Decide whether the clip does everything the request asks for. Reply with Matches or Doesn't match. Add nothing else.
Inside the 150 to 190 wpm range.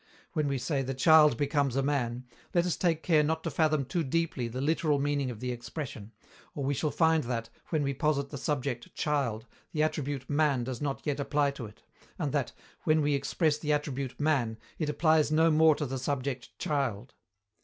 Doesn't match